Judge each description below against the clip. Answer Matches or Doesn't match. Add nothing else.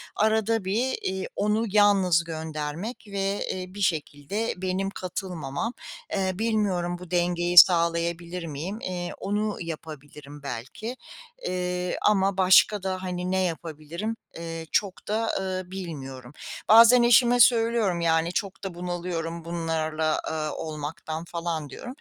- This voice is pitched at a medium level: Matches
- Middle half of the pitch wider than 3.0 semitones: Matches